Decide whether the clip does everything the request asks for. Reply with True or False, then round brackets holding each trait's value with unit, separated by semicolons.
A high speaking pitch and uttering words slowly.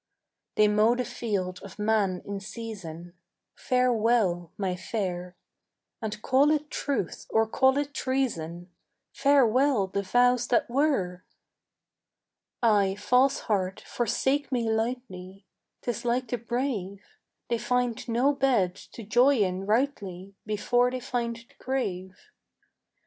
True (225 Hz; 120 wpm)